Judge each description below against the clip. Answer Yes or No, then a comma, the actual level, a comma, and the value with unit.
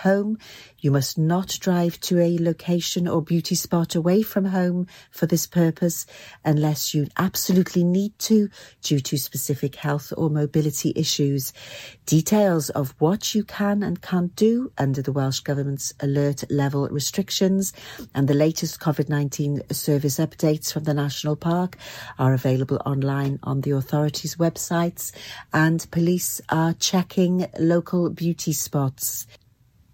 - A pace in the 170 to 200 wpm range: No, average, 140 wpm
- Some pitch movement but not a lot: Yes, average, 3.9 semitones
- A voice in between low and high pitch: Yes, medium, 155 Hz